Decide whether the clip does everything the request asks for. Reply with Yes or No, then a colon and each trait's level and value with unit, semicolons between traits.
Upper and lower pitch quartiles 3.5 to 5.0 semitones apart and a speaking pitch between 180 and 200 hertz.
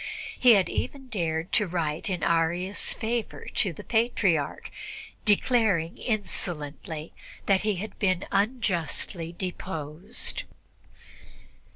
Yes: average, 4.6 semitones; medium, 185 Hz